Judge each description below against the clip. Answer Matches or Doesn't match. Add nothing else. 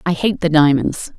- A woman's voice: Matches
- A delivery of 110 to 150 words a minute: Doesn't match